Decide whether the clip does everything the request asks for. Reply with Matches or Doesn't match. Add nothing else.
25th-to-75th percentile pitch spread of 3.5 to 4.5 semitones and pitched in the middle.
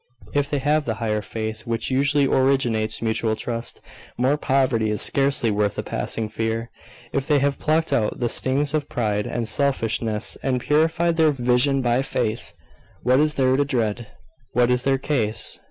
Doesn't match